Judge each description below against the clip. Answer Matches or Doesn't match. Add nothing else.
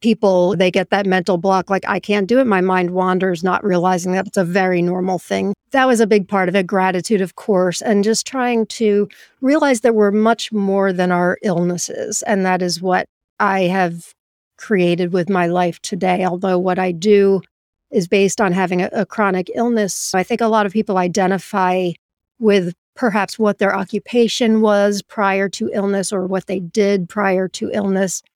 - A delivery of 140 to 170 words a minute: Doesn't match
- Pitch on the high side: Matches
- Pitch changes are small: Matches